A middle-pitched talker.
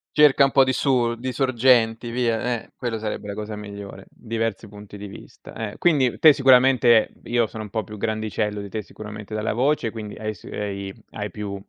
No: low, 110 Hz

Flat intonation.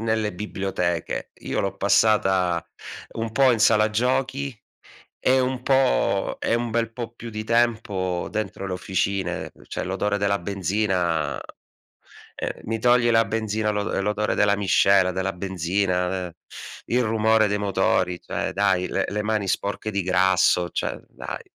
No: average, 3.0 semitones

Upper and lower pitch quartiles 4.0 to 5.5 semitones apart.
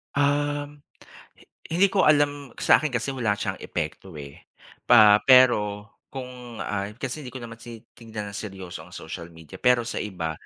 Yes: average, 5.0 semitones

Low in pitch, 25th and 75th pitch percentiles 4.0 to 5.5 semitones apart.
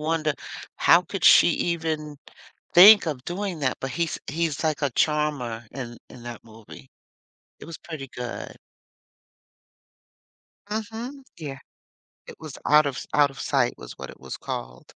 No: medium, 150 Hz; average, 4.4 semitones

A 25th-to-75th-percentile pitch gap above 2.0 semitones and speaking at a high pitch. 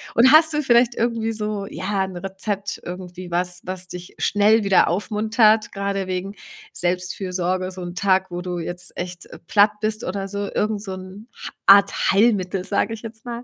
Yes: average, 2.9 semitones; high, 195 Hz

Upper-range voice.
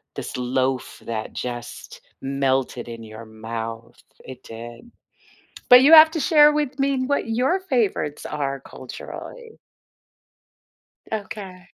No: medium, 145 Hz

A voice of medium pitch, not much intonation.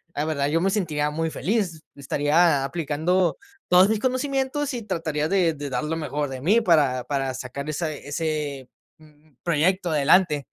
No: medium, 155 Hz; average, 3.8 semitones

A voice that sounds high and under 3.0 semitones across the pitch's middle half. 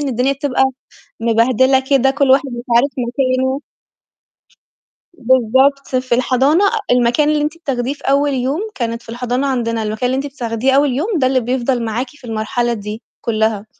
Yes: very high, 255 Hz; narrow, 2.6 semitones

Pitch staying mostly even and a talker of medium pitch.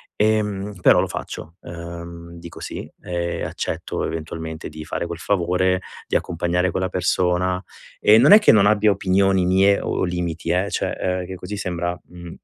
No: narrow, 2.2 semitones; very low, 90 Hz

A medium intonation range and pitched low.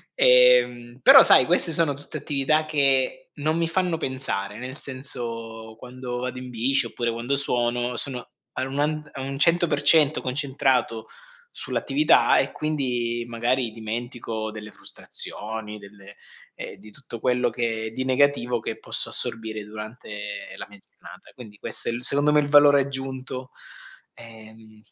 Yes: average, 3.9 semitones; low, 125 Hz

